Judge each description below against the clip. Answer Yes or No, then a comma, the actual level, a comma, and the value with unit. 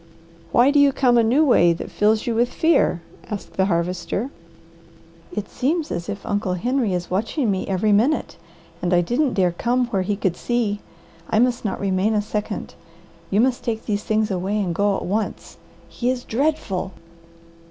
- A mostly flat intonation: No, average, 4.3 semitones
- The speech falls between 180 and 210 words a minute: Yes, average, 185 wpm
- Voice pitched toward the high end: Yes, high, 215 Hz